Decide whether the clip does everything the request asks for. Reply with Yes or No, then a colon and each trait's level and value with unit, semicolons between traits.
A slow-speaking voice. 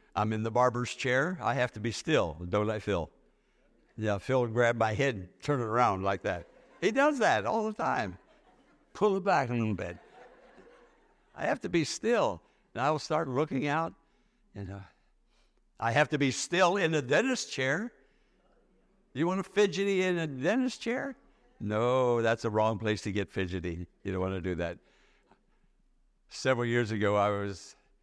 No: average, 180 wpm